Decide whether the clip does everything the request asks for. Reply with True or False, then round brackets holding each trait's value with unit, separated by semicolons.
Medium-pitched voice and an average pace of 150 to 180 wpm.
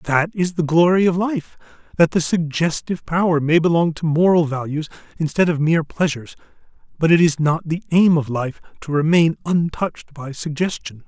True (160 Hz; 175 wpm)